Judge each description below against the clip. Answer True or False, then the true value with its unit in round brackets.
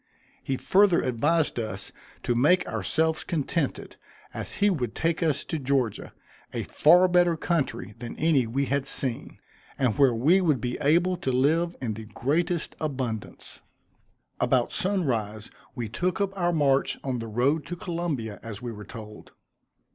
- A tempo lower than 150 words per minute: False (155 wpm)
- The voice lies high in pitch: False (140 Hz)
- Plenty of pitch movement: True (6.1 semitones)